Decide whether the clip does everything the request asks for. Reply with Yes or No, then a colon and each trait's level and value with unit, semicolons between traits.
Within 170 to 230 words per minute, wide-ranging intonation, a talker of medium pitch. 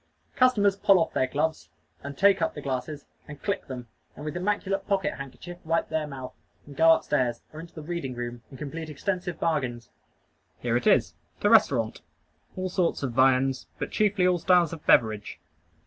Yes: average, 185 wpm; wide, 5.7 semitones; medium, 155 Hz